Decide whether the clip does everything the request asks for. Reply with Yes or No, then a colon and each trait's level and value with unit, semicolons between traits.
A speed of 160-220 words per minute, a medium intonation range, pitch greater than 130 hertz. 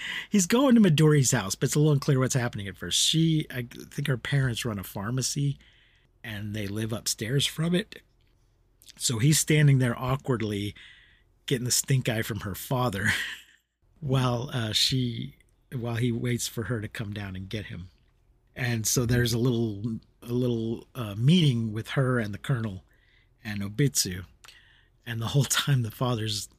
No: average, 170 wpm; average, 3.5 semitones; low, 120 Hz